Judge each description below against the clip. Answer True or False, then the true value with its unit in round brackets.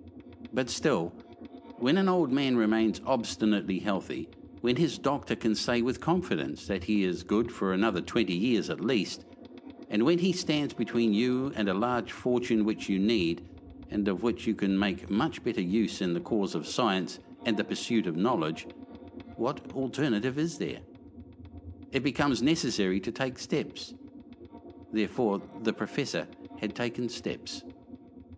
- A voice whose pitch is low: True (115 Hz)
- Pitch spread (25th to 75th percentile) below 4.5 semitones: False (5.2 semitones)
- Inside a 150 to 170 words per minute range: True (155 wpm)